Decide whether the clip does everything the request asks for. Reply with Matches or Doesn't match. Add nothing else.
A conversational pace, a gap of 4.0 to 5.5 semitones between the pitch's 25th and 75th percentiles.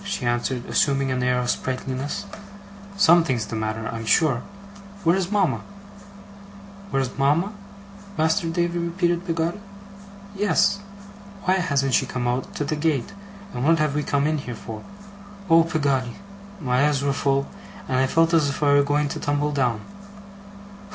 Matches